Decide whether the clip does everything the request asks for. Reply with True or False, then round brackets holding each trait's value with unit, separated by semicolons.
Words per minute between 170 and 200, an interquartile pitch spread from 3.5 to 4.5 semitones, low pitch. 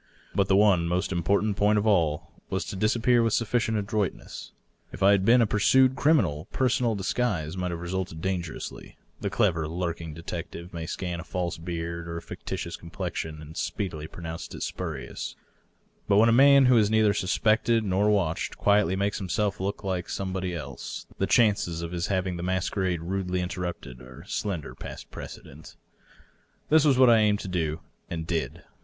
True (180 wpm; 3.9 semitones; 95 Hz)